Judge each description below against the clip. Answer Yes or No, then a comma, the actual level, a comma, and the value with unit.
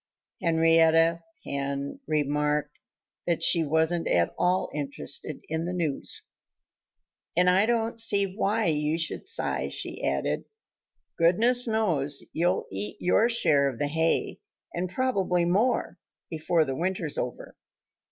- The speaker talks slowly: Yes, slow, 125 wpm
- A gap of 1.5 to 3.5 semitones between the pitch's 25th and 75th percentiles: No, average, 3.9 semitones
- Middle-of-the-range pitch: Yes, medium, 165 Hz